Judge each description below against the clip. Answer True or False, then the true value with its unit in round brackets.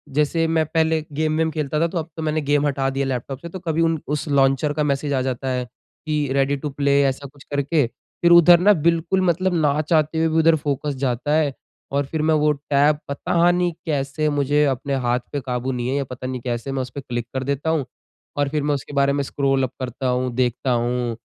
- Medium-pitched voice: True (145 Hz)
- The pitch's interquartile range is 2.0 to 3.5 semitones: True (2.9 semitones)